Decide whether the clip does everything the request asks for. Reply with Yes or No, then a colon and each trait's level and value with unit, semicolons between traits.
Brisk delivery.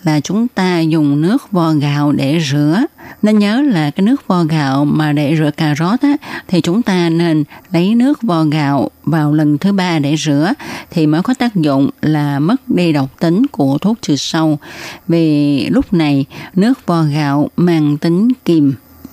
No: average, 180 wpm